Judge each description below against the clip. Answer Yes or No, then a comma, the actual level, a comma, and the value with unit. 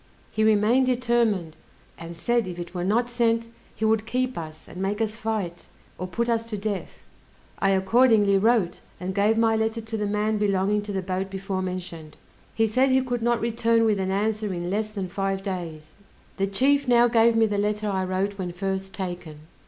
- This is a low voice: No, high, 210 Hz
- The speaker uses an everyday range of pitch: Yes, average, 3.2 semitones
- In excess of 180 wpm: Yes, average, 200 wpm